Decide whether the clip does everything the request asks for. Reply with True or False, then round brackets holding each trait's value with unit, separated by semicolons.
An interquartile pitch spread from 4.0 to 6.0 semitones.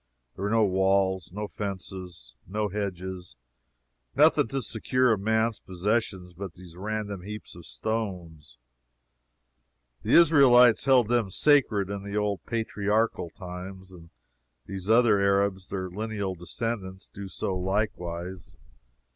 False (2.9 semitones)